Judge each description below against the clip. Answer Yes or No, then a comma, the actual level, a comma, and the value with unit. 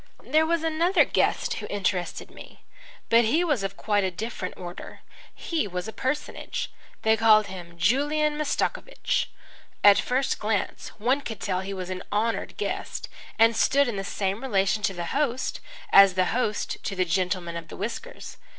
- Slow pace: No, average, 170 wpm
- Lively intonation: Yes, wide, 6.0 semitones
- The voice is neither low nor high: No, high, 215 Hz